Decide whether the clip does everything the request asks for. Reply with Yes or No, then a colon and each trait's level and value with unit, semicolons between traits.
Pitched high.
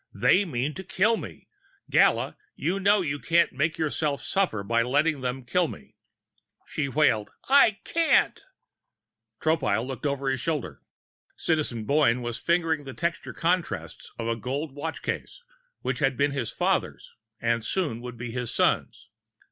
No: medium, 145 Hz